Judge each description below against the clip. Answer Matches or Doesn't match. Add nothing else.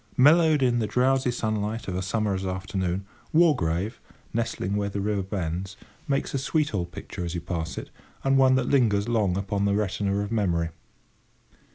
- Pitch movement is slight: Doesn't match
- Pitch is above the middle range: Doesn't match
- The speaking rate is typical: Matches